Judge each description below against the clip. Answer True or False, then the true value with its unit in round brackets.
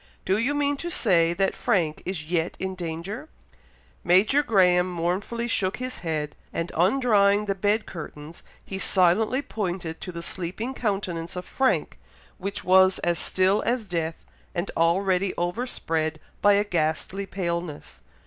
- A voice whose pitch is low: False (185 Hz)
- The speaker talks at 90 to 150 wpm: True (145 wpm)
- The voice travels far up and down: False (3.4 semitones)